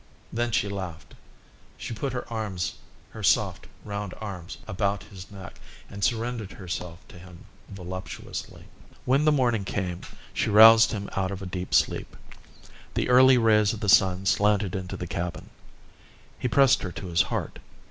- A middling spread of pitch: Yes, average, 3.5 semitones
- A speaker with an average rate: Yes, average, 160 wpm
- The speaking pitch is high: No, low, 100 Hz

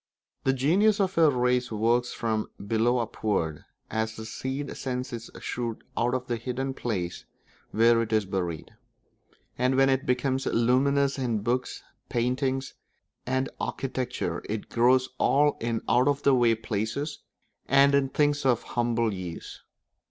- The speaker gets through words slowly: No, average, 145 wpm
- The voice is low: Yes, low, 125 Hz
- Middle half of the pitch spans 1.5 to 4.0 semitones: Yes, average, 2.9 semitones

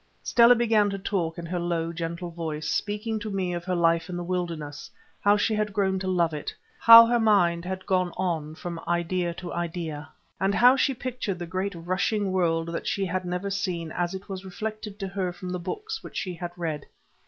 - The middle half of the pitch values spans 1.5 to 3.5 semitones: Yes, average, 2.9 semitones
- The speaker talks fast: Yes, fast, 210 wpm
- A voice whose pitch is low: No, medium, 180 Hz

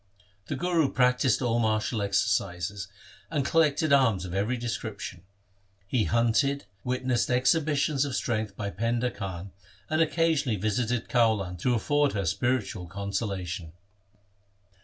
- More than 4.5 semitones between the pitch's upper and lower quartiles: Yes, average, 4.9 semitones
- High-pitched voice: No, low, 115 Hz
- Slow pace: Yes, slow, 125 wpm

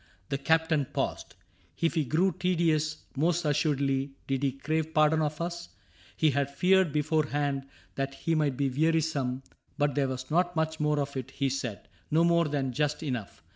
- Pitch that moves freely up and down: No, average, 2.8 semitones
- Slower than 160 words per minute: No, average, 175 wpm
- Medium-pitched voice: Yes, medium, 150 Hz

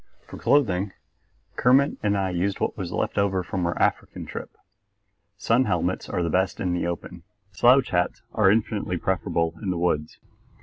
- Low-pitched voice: Yes, very low, 95 Hz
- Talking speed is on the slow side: No, average, 165 wpm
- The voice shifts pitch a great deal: No, narrow, 2.6 semitones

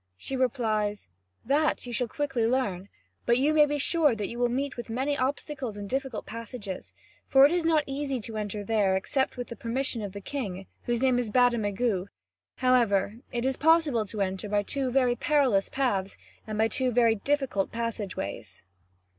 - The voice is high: Yes, high, 240 Hz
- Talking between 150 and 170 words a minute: No, average, 185 wpm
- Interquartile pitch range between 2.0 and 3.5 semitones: No, average, 4.4 semitones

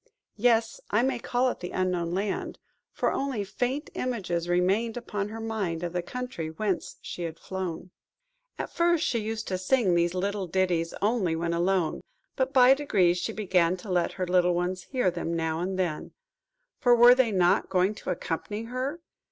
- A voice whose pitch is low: No, high, 190 Hz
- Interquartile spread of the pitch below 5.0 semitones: No, average, 5.3 semitones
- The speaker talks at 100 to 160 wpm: No, average, 175 wpm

